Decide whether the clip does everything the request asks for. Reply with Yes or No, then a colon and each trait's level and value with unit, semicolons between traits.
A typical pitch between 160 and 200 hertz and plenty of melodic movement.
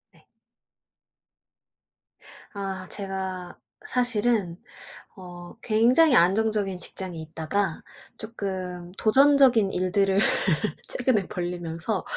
No: high, 195 Hz; average, 3.7 semitones